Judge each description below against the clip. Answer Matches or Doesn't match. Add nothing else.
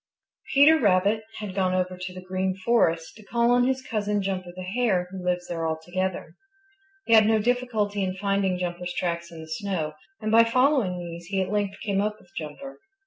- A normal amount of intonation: Matches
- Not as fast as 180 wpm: Doesn't match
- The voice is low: Doesn't match